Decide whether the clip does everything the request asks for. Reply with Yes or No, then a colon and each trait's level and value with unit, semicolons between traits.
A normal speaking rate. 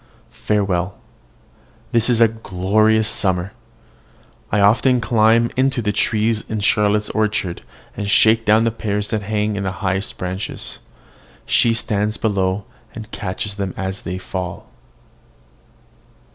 No: slow, 130 wpm